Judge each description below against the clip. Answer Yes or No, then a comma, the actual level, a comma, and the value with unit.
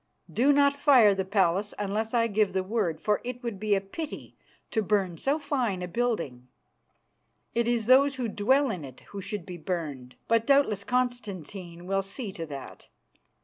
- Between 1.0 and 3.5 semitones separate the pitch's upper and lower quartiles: No, average, 4.8 semitones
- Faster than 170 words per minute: Yes, average, 180 wpm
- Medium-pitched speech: No, high, 210 Hz